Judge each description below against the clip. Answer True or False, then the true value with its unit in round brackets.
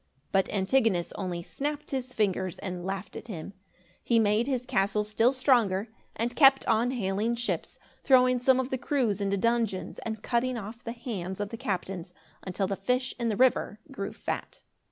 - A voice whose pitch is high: True (220 Hz)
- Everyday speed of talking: True (175 wpm)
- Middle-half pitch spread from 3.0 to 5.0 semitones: True (4.4 semitones)